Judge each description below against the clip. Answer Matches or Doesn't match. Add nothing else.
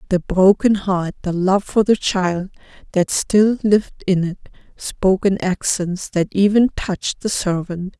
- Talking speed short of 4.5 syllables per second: Matches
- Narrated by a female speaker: Matches